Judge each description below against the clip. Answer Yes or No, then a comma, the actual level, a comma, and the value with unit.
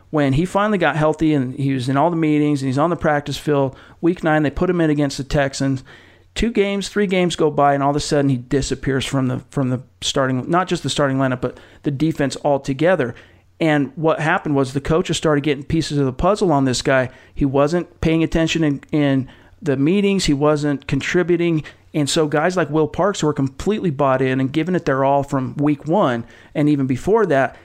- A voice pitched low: No, medium, 145 Hz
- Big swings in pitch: No, average, 3.0 semitones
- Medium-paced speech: No, fast, 220 wpm